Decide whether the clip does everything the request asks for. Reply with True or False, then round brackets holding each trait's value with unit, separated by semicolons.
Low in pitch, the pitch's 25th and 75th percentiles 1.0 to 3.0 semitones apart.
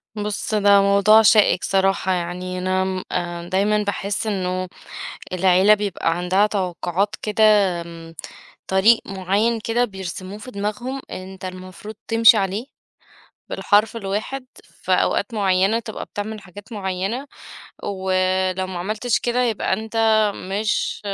False (195 Hz; 2.4 semitones)